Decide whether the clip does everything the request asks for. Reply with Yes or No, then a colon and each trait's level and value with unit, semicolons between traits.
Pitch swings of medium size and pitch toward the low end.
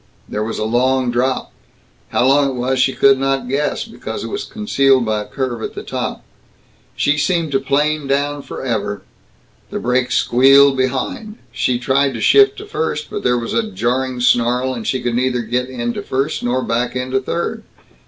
No: narrow, 2.3 semitones; low, 130 Hz